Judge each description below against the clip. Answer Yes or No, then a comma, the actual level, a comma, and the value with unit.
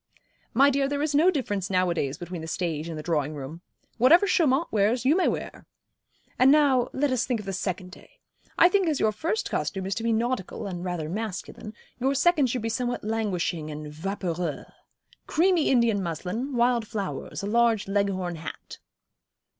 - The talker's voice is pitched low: No, high, 215 Hz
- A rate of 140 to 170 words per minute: No, average, 180 wpm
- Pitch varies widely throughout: Yes, wide, 6.7 semitones